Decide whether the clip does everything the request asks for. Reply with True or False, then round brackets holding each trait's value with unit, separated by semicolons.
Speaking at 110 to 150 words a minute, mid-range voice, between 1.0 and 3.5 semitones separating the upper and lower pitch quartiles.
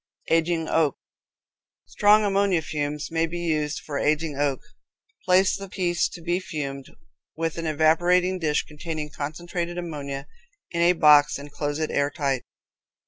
True (140 wpm; 160 Hz; 2.8 semitones)